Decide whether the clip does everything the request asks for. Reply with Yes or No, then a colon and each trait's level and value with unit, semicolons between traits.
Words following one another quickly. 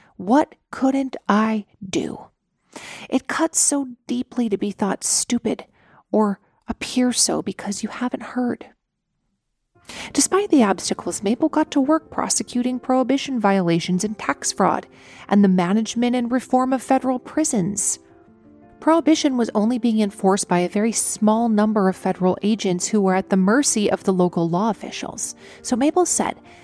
No: average, 150 wpm